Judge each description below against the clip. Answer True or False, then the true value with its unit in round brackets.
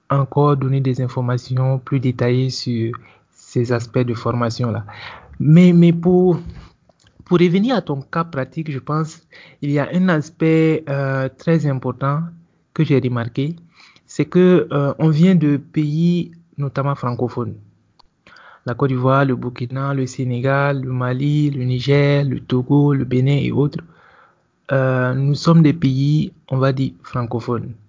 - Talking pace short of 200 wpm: True (150 wpm)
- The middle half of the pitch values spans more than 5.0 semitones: False (3.8 semitones)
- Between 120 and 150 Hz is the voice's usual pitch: True (140 Hz)